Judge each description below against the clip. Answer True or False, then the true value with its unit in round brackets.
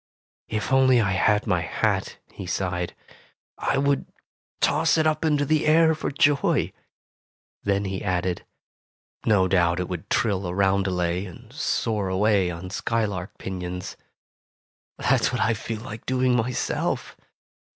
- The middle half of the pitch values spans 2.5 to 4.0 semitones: False (5.2 semitones)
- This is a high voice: False (100 Hz)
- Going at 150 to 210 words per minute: False (140 wpm)